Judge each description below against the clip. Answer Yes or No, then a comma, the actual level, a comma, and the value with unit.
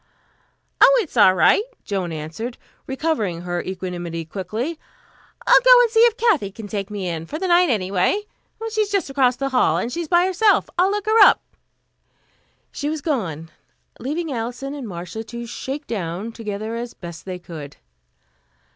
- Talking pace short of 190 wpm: Yes, average, 165 wpm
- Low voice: No, high, 235 Hz